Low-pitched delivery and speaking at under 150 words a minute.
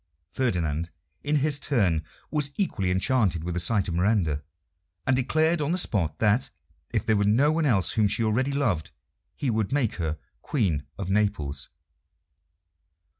No: low, 105 Hz; average, 160 wpm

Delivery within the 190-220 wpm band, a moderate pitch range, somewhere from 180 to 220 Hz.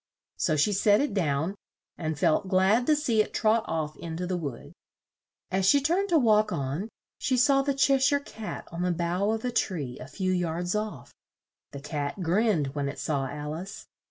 No: average, 200 wpm; wide, 6.2 semitones; medium, 185 Hz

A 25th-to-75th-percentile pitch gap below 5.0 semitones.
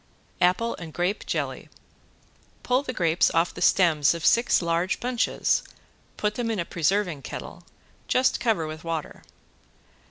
No: wide, 5.5 semitones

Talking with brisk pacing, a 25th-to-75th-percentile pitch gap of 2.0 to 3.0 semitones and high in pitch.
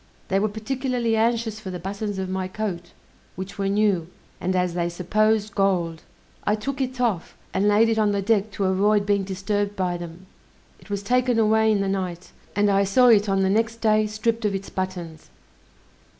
No: average, 195 wpm; narrow, 2.6 semitones; high, 205 Hz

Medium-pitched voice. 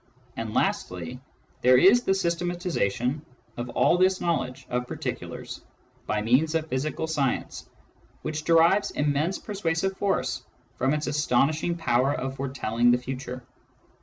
Yes: medium, 145 Hz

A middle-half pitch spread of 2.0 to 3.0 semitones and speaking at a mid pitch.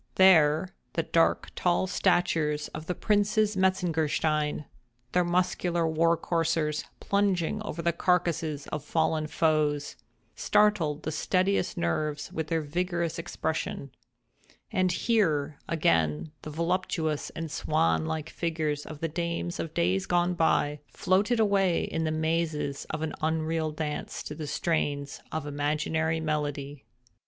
Yes: average, 2.7 semitones; medium, 160 Hz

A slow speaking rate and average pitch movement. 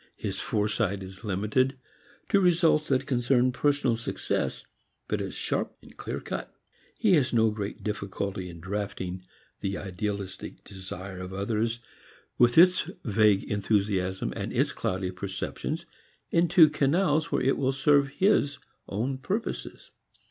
No: slow, 125 wpm; wide, 6.2 semitones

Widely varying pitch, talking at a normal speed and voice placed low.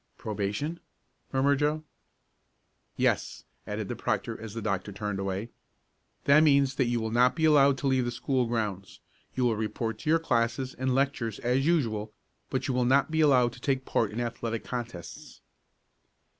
No: average, 3.7 semitones; average, 170 wpm; low, 120 Hz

